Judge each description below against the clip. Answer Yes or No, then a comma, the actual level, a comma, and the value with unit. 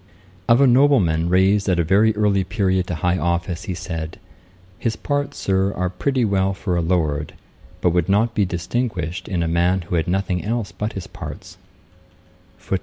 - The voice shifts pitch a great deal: No, average, 3.3 semitones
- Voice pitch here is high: No, very low, 95 Hz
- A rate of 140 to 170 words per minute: No, average, 180 wpm